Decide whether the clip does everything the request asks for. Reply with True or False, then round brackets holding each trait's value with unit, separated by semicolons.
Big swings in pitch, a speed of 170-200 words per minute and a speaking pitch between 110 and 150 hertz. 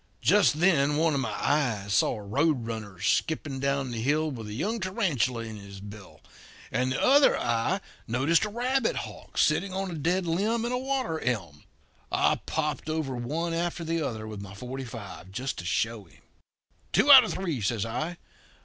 True (7.3 semitones; 185 wpm; 140 Hz)